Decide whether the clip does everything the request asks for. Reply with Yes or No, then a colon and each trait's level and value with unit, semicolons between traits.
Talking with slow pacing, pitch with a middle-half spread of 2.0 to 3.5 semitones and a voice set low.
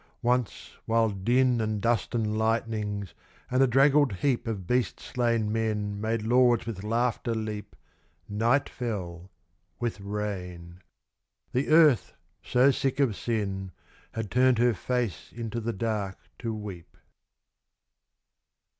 Yes: slow, 125 wpm; average, 2.9 semitones; low, 115 Hz